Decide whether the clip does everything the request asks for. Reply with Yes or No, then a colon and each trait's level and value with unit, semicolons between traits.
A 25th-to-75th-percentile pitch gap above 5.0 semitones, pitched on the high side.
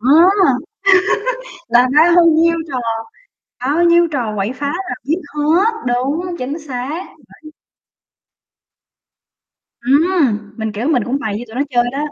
Yes: wide, 5.5 semitones; very high, 280 Hz